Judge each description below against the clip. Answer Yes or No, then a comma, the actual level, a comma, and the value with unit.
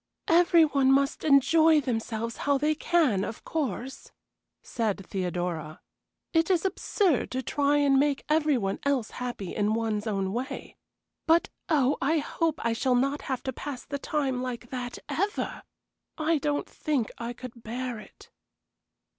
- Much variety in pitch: No, average, 4.5 semitones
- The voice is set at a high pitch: Yes, very high, 265 Hz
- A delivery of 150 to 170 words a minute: Yes, average, 155 wpm